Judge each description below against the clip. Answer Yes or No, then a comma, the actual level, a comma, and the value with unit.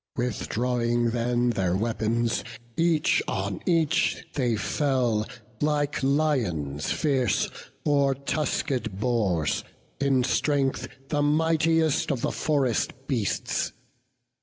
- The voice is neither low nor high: No, low, 130 Hz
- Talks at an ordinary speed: No, slow, 95 wpm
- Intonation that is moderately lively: Yes, average, 4.3 semitones